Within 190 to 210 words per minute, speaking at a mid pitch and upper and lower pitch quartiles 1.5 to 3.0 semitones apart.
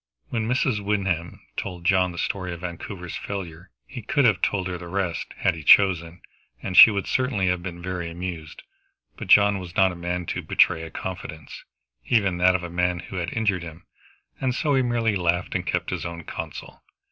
No: fast, 205 wpm; very low, 90 Hz; average, 2.7 semitones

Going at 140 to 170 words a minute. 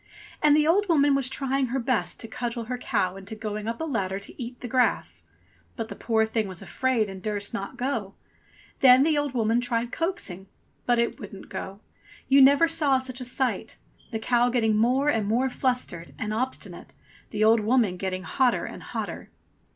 No: average, 195 wpm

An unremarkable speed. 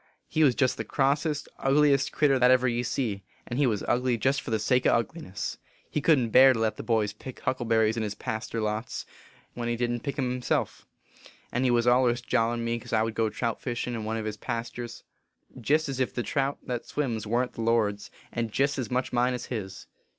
No: fast, 230 wpm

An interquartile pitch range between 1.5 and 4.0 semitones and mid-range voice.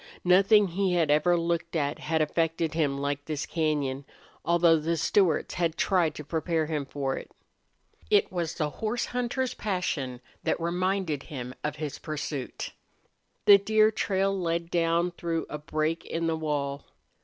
Yes: average, 3.1 semitones; medium, 165 Hz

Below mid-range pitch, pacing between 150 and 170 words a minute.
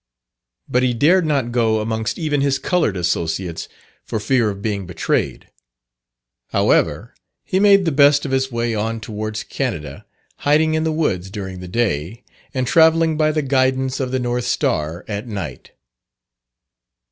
Yes: low, 120 Hz; average, 155 wpm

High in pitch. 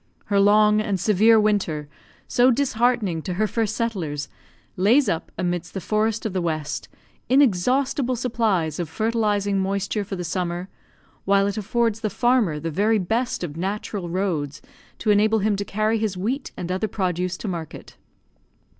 Yes: high, 205 Hz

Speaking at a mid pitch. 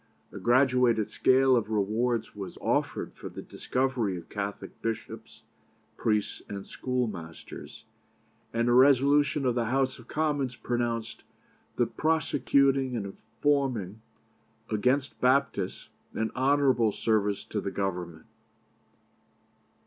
No: low, 120 Hz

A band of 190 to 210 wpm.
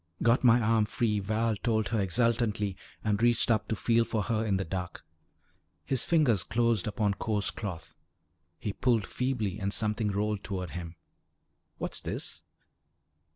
No: average, 155 wpm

